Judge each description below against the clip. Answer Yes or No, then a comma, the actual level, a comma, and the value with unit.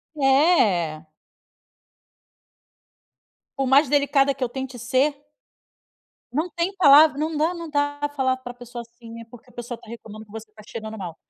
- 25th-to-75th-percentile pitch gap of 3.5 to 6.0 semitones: Yes, average, 3.9 semitones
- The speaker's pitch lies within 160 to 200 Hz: No, very high, 260 Hz